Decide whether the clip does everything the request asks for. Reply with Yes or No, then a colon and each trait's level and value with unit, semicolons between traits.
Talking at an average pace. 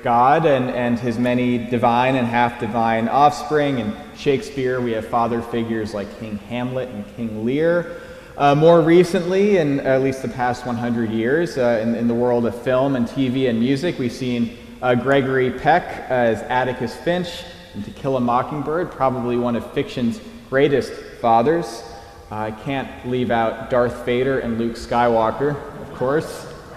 Yes: average, 165 wpm